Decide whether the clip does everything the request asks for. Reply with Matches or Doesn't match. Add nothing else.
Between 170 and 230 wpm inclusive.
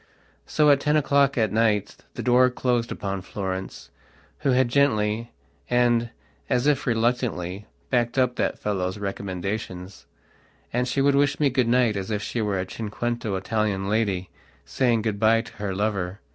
Doesn't match